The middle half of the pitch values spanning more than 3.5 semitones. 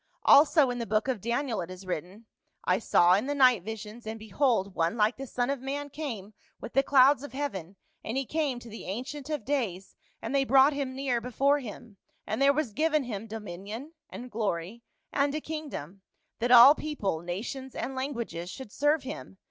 Yes: average, 4.9 semitones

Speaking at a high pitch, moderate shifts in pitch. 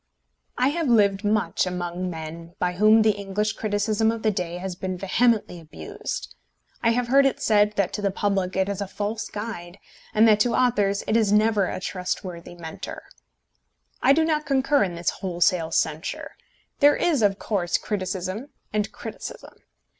Yes: high, 205 Hz; average, 3.7 semitones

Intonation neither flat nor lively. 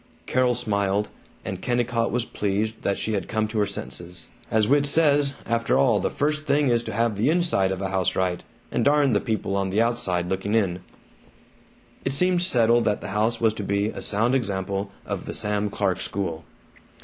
Yes: average, 4.0 semitones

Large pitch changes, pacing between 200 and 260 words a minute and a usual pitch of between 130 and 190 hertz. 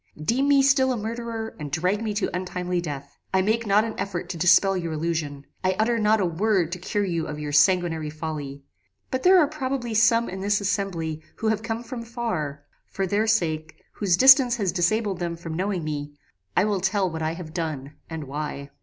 Yes: wide, 5.7 semitones; fast, 205 wpm; medium, 185 Hz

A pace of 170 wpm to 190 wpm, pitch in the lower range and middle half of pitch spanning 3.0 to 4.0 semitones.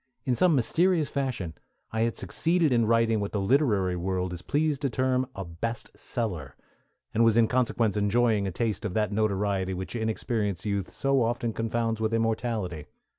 Yes: average, 175 wpm; low, 115 Hz; average, 3.5 semitones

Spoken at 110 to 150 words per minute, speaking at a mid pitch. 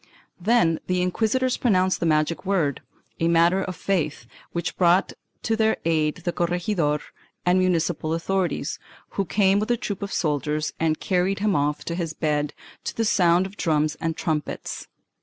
No: average, 175 wpm; medium, 175 Hz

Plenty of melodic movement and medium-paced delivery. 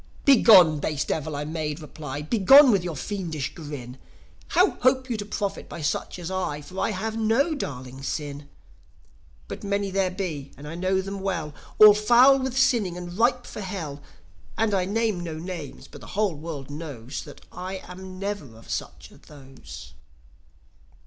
Yes: wide, 5.8 semitones; average, 175 wpm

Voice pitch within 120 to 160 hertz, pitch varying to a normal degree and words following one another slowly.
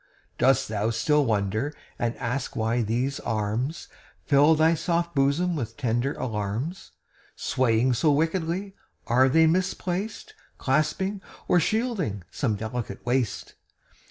No: low, 135 Hz; wide, 6.1 semitones; slow, 120 wpm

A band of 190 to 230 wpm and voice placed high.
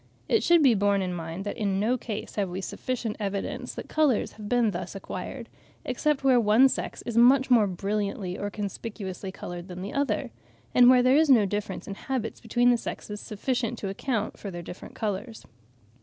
Yes: average, 195 wpm; high, 215 Hz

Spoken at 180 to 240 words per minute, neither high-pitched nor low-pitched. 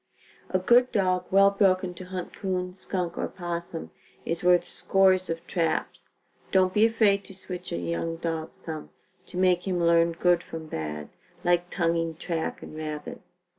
No: average, 165 wpm; medium, 180 Hz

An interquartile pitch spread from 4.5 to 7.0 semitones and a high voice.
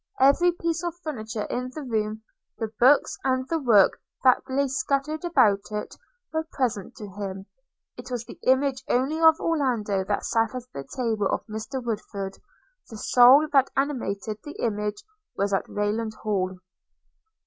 Yes: average, 4.8 semitones; high, 240 Hz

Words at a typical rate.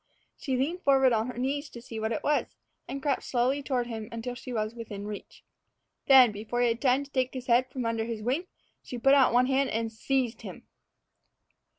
No: fast, 215 wpm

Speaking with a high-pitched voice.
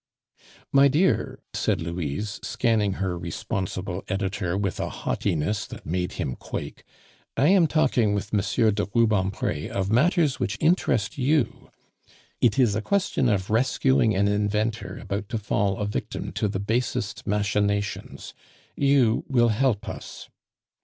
No: low, 105 Hz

